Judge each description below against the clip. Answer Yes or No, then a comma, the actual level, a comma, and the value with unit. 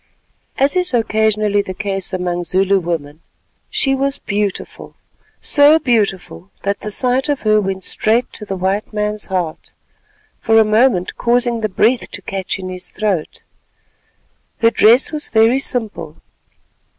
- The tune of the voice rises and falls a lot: No, average, 4.0 semitones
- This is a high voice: Yes, high, 215 Hz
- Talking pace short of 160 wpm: Yes, average, 140 wpm